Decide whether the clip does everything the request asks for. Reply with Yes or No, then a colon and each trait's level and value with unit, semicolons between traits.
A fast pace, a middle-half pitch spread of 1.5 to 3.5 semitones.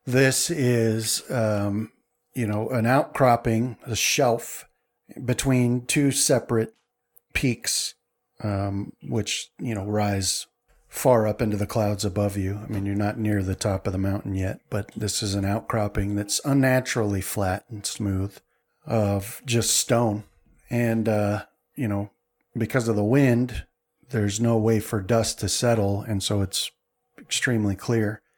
No: average, 145 wpm; average, 2.7 semitones